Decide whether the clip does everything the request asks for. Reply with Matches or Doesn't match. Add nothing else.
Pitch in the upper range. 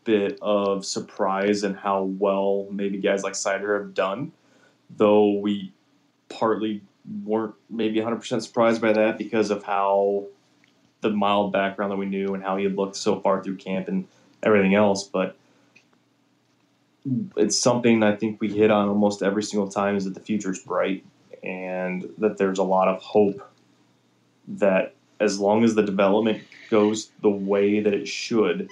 Doesn't match